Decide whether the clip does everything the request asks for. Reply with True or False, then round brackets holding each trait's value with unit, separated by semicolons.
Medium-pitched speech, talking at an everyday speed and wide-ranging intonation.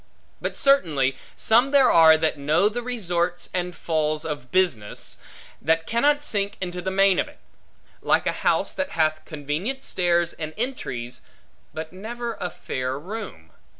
True (175 Hz; 150 wpm; 6.0 semitones)